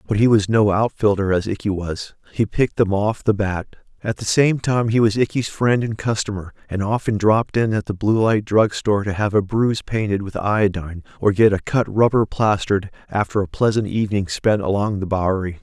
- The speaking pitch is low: Yes, low, 105 Hz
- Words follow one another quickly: Yes, fast, 210 wpm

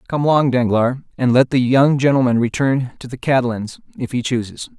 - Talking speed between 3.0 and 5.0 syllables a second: No, 5.6 syllables/s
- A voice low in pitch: Yes, low, 130 Hz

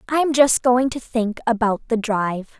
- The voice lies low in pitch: No, high, 235 Hz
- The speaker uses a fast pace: No, average, 185 wpm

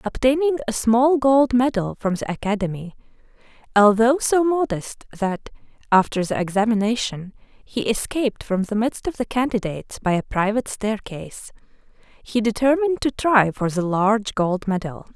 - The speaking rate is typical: Yes, average, 145 wpm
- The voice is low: No, high, 225 Hz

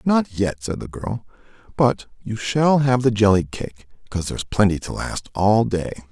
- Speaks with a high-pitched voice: No, low, 110 Hz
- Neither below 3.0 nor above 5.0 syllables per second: Yes, 4.7 syllables/s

